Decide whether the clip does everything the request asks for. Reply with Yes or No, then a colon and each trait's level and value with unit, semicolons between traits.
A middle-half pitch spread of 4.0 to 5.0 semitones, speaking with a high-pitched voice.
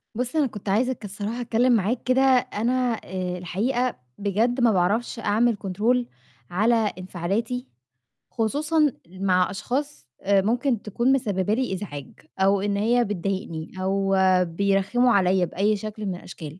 Yes: average, 4.3 semitones; high, 210 Hz